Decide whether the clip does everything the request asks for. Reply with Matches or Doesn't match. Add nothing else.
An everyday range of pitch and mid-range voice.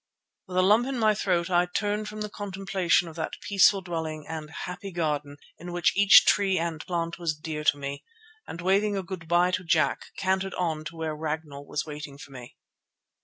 Matches